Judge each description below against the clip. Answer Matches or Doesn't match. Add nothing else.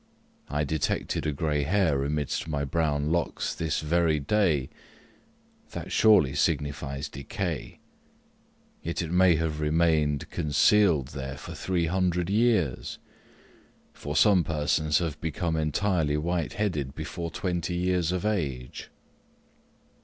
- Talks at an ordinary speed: Doesn't match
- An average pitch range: Matches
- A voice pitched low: Matches